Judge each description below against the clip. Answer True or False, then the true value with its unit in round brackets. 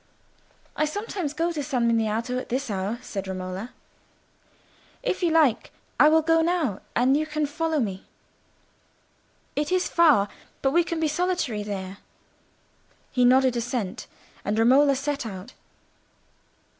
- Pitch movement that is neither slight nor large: False (6.1 semitones)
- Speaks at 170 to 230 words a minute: False (140 wpm)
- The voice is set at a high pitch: True (270 Hz)